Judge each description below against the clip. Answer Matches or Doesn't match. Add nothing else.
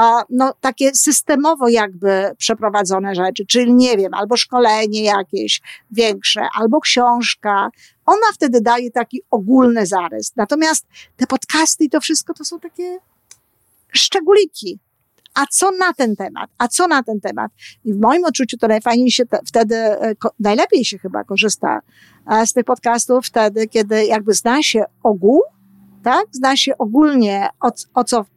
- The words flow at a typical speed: Matches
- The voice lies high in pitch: Matches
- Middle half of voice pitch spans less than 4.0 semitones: Doesn't match